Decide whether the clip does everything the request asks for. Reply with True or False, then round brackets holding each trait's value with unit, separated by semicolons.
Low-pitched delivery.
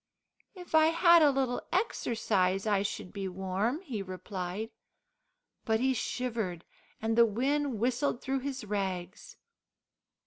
False (225 Hz)